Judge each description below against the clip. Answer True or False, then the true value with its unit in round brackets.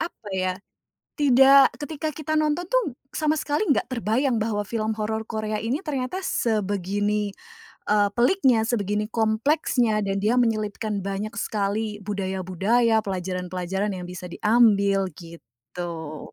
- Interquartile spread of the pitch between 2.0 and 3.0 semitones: False (4.0 semitones)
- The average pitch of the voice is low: False (215 Hz)